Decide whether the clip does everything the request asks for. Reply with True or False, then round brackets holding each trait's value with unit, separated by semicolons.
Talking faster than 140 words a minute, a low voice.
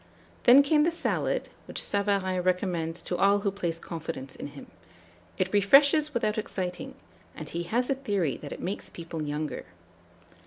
False (165 wpm; 195 Hz)